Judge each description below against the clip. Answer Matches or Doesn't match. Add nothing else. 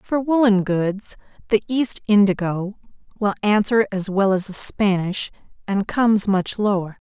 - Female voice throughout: Matches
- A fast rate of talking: Doesn't match